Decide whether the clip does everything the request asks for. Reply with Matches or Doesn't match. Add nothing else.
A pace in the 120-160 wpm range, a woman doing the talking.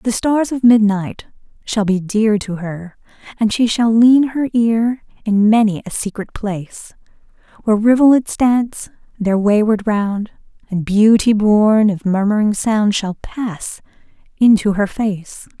Matches